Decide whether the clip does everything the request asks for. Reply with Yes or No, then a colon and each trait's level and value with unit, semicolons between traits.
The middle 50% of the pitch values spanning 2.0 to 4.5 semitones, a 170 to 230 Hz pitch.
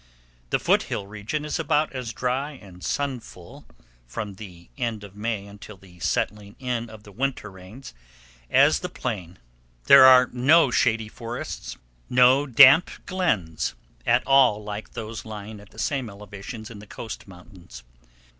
No: average, 4.2 semitones; low, 110 Hz